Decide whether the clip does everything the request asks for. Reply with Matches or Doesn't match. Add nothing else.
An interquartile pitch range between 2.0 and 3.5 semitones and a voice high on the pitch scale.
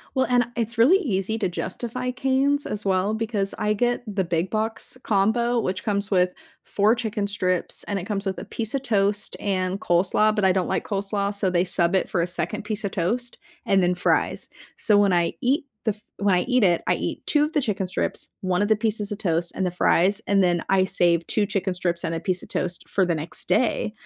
Matches